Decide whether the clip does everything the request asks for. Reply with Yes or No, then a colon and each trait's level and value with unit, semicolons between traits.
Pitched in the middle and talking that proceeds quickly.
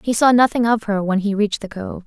No: high, 210 Hz; fast, 290 wpm